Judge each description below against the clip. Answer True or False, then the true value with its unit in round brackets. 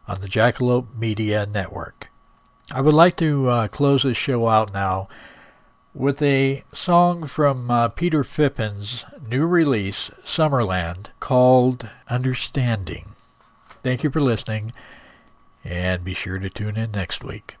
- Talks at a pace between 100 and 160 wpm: True (135 wpm)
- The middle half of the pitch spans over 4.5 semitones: True (5.0 semitones)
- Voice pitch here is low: True (120 Hz)